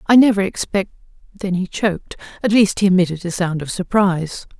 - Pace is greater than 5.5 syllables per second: Yes, 5.7 syllables/s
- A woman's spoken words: Yes, female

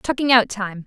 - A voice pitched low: No, high, 225 Hz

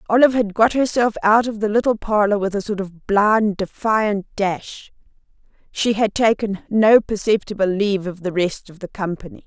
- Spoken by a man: No, female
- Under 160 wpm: No, average, 175 wpm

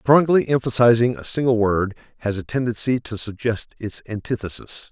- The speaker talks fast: No, average, 145 wpm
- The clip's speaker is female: No, male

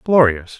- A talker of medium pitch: No, low, 125 Hz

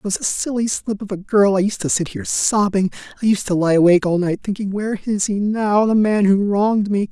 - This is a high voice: Yes, high, 200 Hz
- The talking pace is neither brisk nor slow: No, fast, 260 wpm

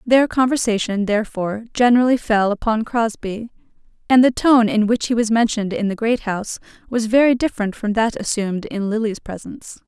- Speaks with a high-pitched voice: Yes, high, 225 Hz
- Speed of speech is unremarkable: Yes, average, 170 wpm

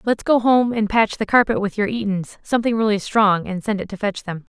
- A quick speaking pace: Yes, fast, 225 wpm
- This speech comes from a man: No, female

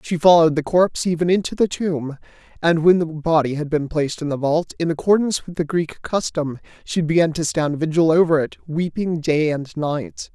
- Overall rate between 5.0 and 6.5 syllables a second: Yes, 5.3 syllables/s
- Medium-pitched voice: Yes, medium, 160 Hz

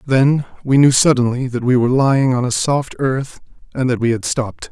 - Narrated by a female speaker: No, male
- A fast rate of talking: Yes, fast, 215 wpm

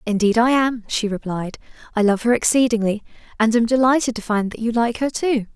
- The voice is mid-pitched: No, high, 230 Hz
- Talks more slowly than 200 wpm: No, fast, 205 wpm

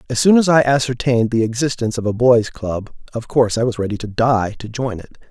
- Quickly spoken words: Yes, fast, 235 wpm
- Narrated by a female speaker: No, male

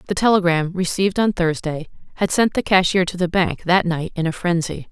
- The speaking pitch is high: No, medium, 180 Hz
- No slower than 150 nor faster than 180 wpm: No, fast, 205 wpm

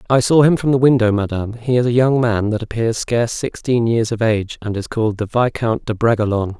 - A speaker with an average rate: No, fast, 235 wpm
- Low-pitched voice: Yes, low, 115 Hz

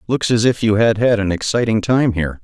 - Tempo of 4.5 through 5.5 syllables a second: No, 5.7 syllables/s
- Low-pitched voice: Yes, low, 110 Hz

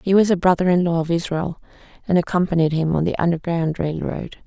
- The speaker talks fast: Yes, fast, 215 wpm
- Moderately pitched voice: Yes, medium, 170 Hz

